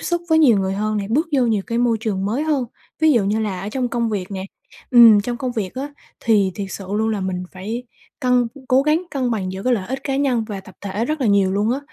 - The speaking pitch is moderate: No, high, 225 Hz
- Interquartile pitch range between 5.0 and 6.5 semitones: No, average, 4.2 semitones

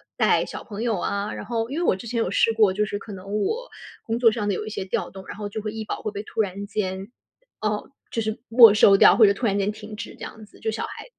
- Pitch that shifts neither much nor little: No, narrow, 1.9 semitones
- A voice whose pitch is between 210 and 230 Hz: Yes, high, 215 Hz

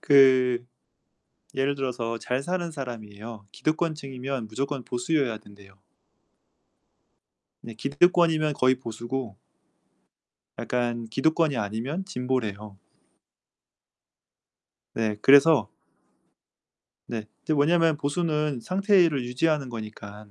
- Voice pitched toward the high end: No, low, 130 Hz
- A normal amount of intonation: Yes, average, 4.9 semitones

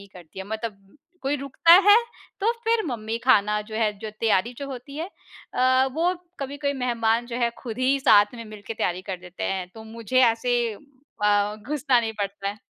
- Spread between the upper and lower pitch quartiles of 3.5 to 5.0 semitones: Yes, average, 4.2 semitones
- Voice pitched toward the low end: No, high, 230 Hz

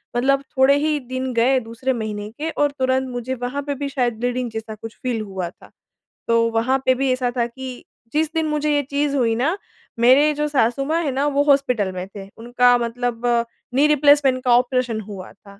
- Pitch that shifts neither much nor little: Yes, average, 3.4 semitones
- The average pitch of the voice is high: Yes, very high, 255 Hz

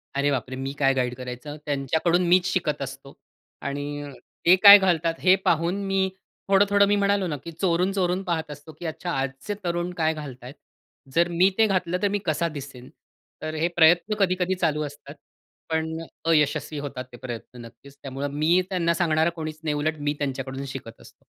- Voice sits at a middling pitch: Yes, medium, 155 Hz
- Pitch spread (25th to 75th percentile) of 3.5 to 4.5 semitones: Yes, average, 4.1 semitones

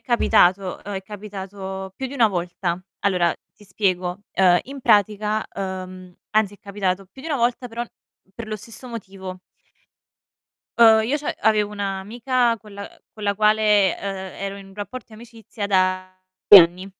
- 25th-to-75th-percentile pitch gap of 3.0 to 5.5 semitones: No, narrow, 2.6 semitones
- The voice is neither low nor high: No, high, 200 Hz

